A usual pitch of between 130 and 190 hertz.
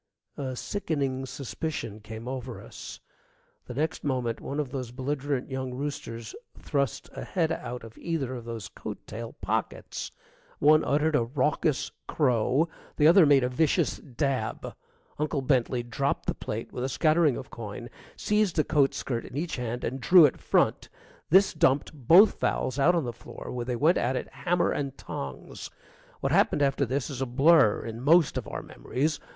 Yes: low, 135 Hz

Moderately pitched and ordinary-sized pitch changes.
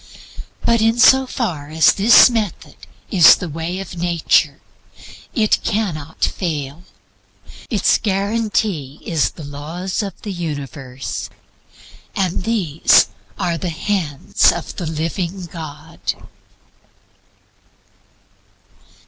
Yes: medium, 175 Hz; average, 4.7 semitones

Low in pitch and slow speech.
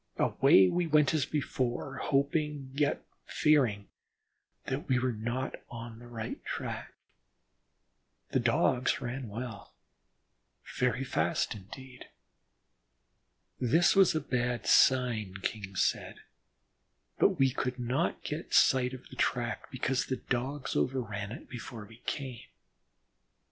Yes: low, 125 Hz; slow, 120 wpm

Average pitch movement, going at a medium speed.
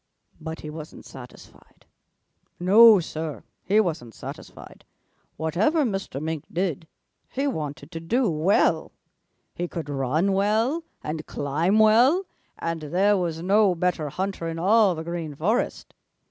No: average, 4.7 semitones; slow, 130 wpm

